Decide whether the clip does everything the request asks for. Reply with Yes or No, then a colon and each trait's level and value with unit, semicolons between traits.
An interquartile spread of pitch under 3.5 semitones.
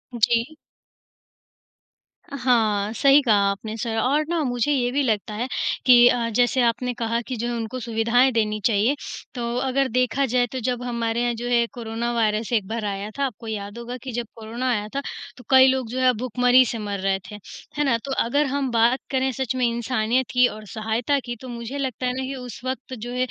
Yes: narrow, 2.5 semitones